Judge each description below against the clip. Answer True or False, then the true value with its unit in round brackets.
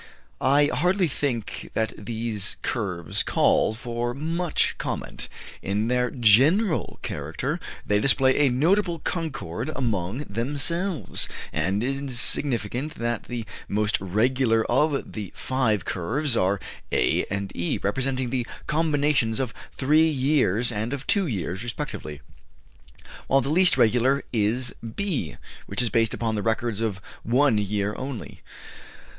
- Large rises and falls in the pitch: False (4.9 semitones)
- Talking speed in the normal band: False (130 wpm)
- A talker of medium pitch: False (120 Hz)